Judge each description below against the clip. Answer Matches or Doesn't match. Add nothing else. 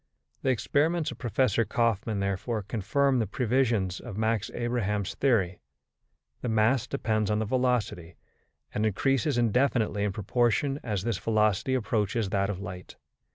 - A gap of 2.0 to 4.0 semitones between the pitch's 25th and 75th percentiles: Matches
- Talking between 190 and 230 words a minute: Doesn't match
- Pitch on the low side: Matches